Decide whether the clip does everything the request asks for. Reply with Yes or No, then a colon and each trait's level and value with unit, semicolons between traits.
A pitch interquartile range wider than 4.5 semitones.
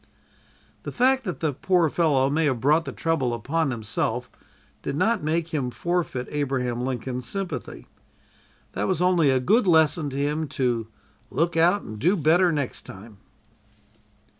Yes: average, 5.0 semitones